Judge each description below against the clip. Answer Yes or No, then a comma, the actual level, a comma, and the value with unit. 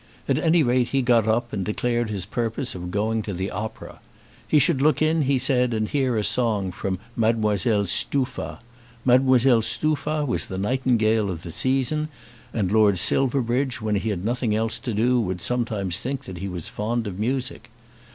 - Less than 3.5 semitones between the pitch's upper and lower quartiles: No, average, 3.8 semitones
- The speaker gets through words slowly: No, average, 180 wpm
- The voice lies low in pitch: Yes, low, 115 Hz